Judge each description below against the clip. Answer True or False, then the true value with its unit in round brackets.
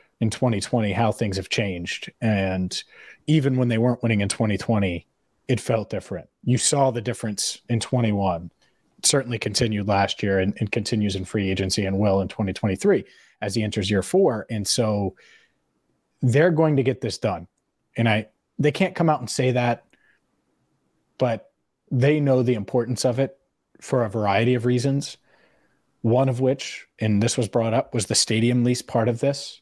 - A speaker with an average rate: True (175 wpm)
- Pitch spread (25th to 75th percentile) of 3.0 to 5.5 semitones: True (3.7 semitones)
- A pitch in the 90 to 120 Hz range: True (115 Hz)